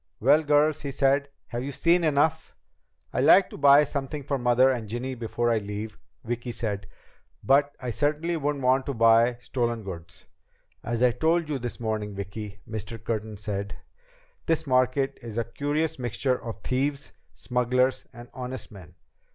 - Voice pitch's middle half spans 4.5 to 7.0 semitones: No, average, 3.9 semitones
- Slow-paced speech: No, average, 165 wpm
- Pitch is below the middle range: Yes, low, 125 Hz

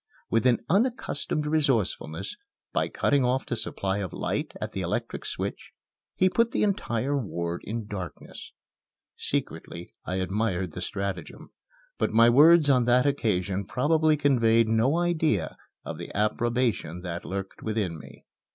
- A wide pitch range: Yes, wide, 6.9 semitones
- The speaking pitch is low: Yes, low, 115 Hz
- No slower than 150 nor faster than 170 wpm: No, average, 140 wpm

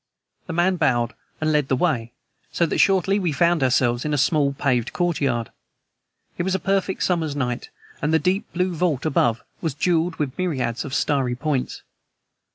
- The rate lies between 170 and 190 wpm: Yes, average, 175 wpm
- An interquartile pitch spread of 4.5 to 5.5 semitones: Yes, average, 5.2 semitones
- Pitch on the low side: No, medium, 150 Hz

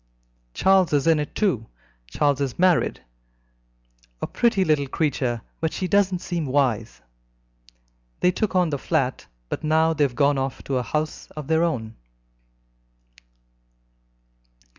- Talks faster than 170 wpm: No, average, 140 wpm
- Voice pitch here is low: No, medium, 150 Hz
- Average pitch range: Yes, average, 4.3 semitones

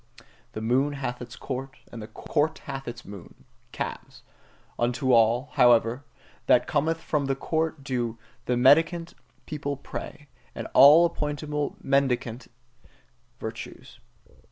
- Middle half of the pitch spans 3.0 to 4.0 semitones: Yes, average, 3.6 semitones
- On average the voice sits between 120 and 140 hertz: Yes, low, 135 Hz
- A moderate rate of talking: No, slow, 125 wpm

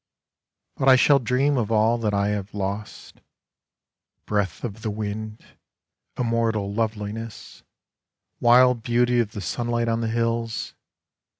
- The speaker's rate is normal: No, slow, 130 wpm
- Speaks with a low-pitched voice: Yes, low, 115 Hz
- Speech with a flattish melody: Yes, narrow, 2.2 semitones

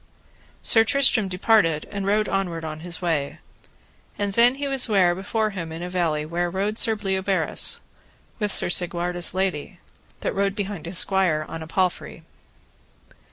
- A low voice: No, high, 190 Hz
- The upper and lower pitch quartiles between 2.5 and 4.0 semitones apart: Yes, average, 3.2 semitones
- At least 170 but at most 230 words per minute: No, average, 160 wpm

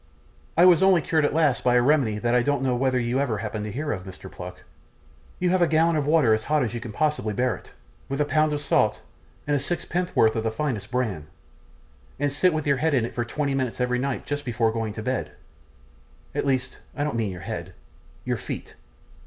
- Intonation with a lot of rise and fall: No, average, 4.9 semitones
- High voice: No, low, 130 Hz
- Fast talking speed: Yes, fast, 225 wpm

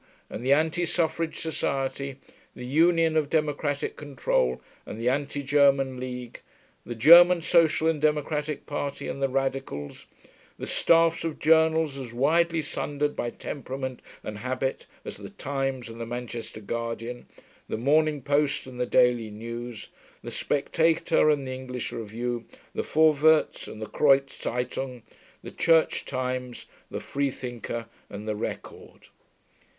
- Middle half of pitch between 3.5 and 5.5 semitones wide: Yes, average, 3.8 semitones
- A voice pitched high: No, low, 135 Hz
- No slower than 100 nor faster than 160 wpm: Yes, average, 140 wpm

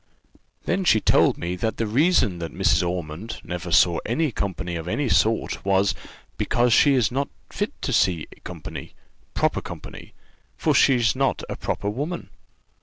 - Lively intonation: Yes, wide, 7.2 semitones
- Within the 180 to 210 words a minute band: No, average, 160 wpm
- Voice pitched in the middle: No, low, 110 Hz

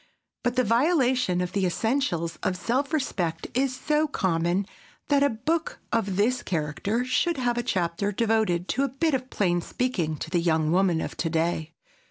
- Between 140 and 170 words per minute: No, average, 180 wpm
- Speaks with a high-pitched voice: Yes, high, 210 Hz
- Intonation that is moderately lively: No, wide, 6.8 semitones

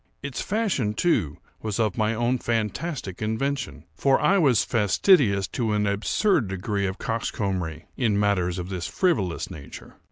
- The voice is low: Yes, low, 110 Hz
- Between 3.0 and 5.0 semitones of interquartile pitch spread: No, wide, 5.4 semitones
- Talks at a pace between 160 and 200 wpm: No, average, 150 wpm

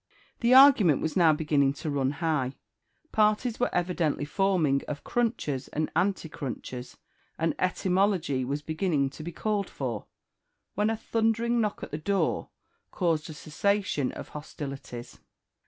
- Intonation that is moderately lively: No, wide, 6.0 semitones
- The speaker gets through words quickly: No, average, 140 wpm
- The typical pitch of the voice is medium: Yes, medium, 160 Hz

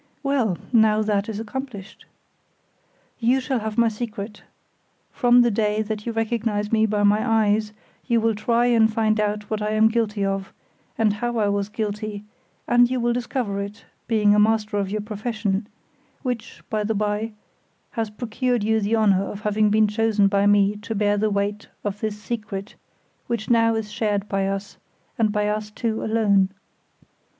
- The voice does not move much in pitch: Yes, narrow, 1.6 semitones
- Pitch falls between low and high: No, high, 215 Hz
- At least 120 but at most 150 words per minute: No, average, 175 wpm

